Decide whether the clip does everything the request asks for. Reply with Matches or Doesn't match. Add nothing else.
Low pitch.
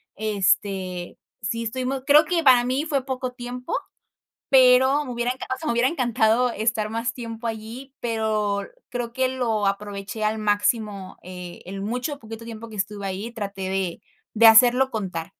Doesn't match